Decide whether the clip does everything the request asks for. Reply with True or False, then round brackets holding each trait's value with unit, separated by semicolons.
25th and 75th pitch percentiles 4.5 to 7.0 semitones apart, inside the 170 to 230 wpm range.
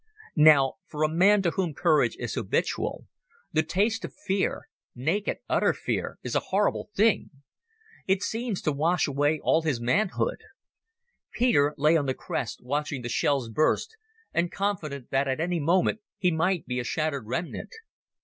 False (5.2 semitones; 150 wpm)